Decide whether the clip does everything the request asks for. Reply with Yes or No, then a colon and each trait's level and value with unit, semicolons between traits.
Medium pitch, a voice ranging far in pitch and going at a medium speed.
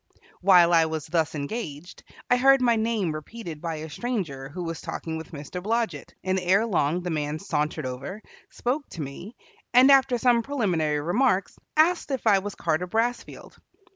Yes: medium, 180 Hz; wide, 6.8 semitones; average, 170 wpm